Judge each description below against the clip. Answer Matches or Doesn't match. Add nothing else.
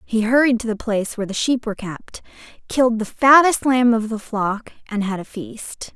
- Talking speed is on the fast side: Matches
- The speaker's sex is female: Matches